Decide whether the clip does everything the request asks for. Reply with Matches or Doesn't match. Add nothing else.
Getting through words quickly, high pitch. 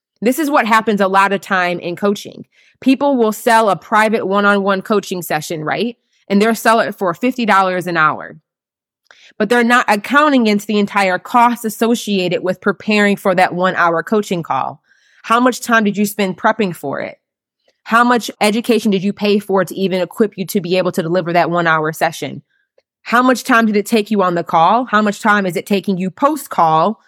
Matches